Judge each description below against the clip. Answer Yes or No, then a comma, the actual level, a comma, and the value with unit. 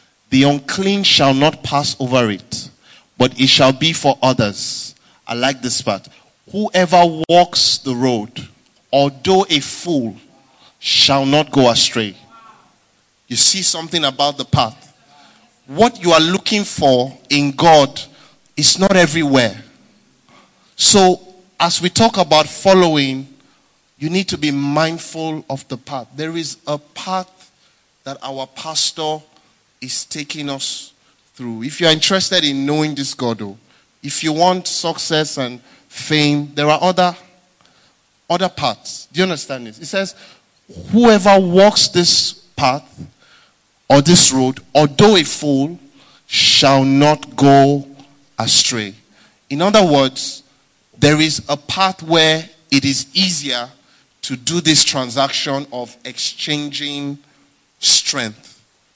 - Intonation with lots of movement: No, average, 4.5 semitones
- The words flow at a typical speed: No, slow, 130 wpm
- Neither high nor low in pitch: Yes, medium, 145 Hz